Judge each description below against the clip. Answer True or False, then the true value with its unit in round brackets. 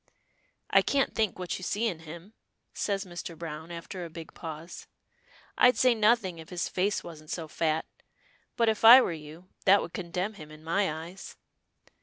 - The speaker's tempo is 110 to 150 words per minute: False (180 wpm)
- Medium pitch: True (175 Hz)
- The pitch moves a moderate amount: True (4.0 semitones)